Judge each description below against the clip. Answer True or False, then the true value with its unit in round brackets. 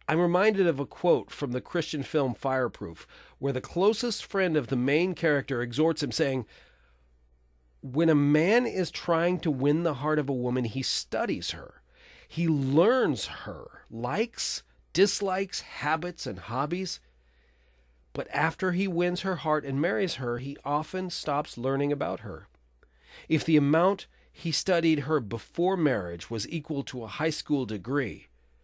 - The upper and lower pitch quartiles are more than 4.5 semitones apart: True (5.3 semitones)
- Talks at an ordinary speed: True (155 wpm)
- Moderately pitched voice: True (145 Hz)